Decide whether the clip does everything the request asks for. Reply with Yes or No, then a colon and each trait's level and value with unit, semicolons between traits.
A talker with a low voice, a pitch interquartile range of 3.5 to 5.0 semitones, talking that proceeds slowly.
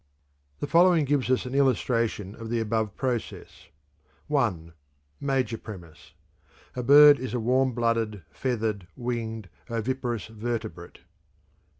No: low, 115 Hz; average, 3.0 semitones; slow, 120 wpm